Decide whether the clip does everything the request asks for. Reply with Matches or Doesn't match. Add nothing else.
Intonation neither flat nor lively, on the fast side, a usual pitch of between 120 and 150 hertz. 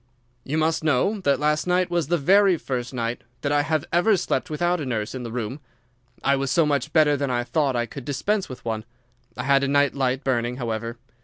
Matches